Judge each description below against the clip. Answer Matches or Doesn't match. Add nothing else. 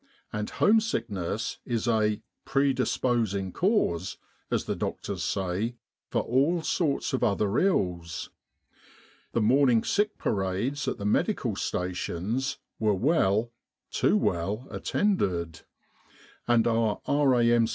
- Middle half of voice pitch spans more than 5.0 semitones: Matches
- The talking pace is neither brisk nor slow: Doesn't match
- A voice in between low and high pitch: Doesn't match